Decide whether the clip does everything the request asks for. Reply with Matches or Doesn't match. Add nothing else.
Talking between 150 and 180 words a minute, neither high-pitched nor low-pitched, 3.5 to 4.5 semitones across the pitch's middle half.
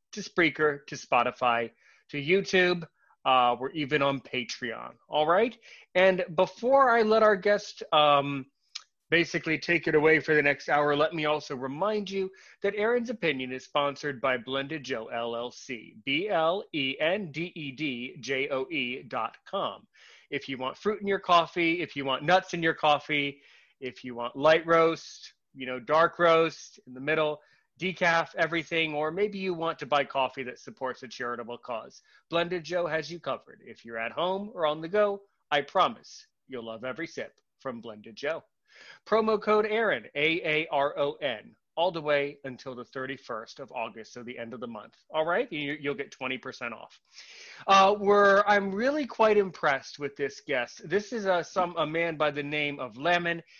Doesn't match